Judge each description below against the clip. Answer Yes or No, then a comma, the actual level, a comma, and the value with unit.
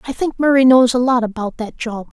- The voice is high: Yes, high, 245 Hz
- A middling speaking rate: No, fast, 245 wpm